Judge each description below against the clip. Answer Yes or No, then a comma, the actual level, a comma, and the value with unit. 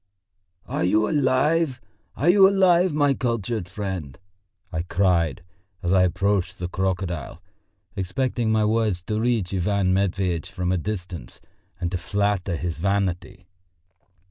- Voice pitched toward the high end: No, very low, 95 Hz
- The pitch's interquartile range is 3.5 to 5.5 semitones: Yes, average, 4.4 semitones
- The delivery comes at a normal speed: No, slow, 130 wpm